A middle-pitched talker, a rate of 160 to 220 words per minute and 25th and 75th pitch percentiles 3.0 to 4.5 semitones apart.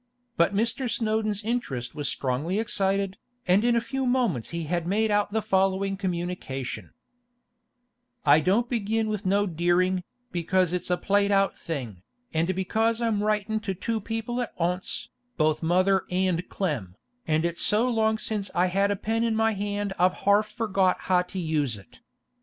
No: high, 195 Hz; average, 170 wpm; average, 3.9 semitones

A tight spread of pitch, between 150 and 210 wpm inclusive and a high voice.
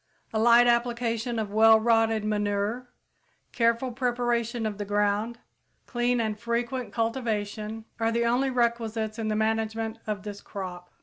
No: narrow, 1.8 semitones; average, 140 wpm; high, 225 Hz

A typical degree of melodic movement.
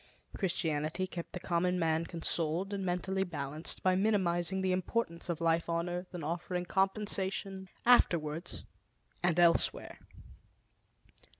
No: narrow, 2.3 semitones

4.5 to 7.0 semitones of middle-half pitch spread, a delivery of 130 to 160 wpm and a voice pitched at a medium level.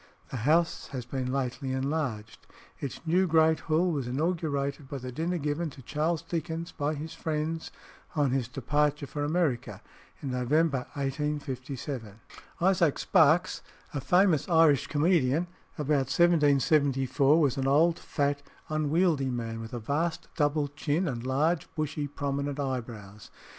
No: average, 3.2 semitones; slow, 135 wpm; medium, 145 Hz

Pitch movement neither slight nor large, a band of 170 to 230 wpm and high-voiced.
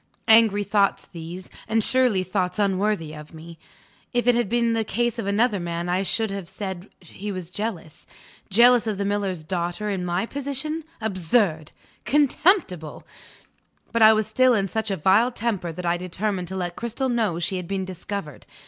Yes: average, 4.1 semitones; average, 175 wpm; high, 200 Hz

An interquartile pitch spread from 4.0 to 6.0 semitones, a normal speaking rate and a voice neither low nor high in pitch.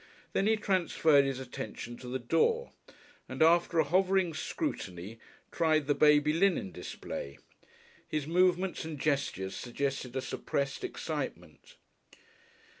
No: wide, 5.4 semitones; slow, 120 wpm; medium, 155 Hz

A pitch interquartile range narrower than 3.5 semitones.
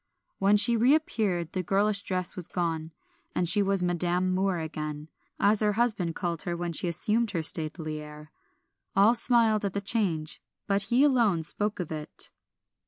No: average, 4.1 semitones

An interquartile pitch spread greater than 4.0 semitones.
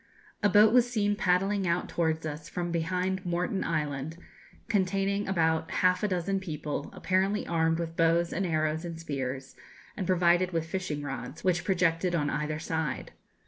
No: average, 2.8 semitones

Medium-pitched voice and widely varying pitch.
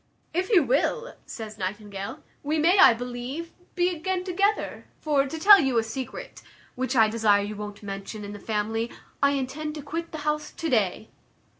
No: very high, 265 Hz; wide, 7.0 semitones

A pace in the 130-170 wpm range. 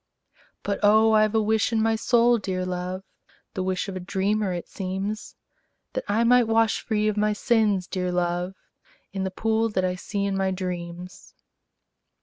No: average, 180 wpm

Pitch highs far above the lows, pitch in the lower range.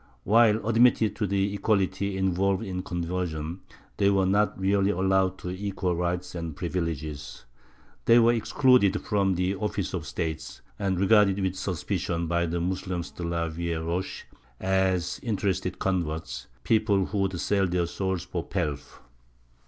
No: average, 2.7 semitones; very low, 95 Hz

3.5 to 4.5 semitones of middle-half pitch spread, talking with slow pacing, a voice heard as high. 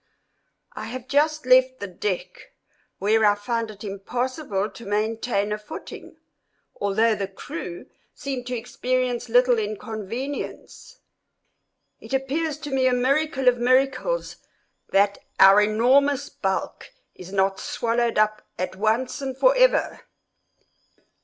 Yes: average, 4.1 semitones; slow, 120 wpm; high, 235 Hz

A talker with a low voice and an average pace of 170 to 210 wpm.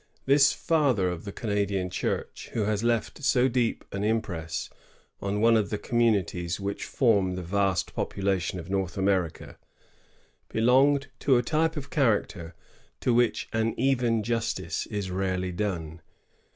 No: low, 105 Hz; average, 145 wpm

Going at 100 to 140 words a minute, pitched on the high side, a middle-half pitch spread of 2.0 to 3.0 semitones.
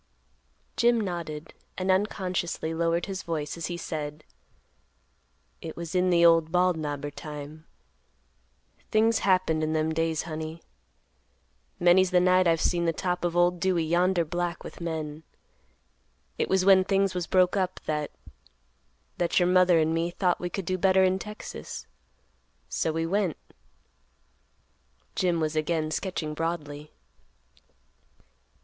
No: slow, 135 wpm; medium, 170 Hz; narrow, 2.6 semitones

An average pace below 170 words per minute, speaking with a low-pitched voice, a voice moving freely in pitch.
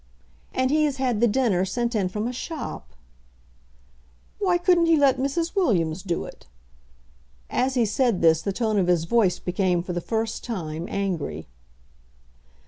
No: average, 160 wpm; high, 225 Hz; wide, 6.6 semitones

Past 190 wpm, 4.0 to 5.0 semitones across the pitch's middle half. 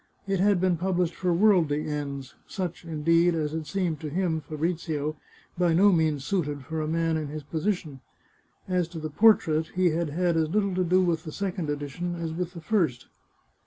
No: average, 200 wpm; average, 2.8 semitones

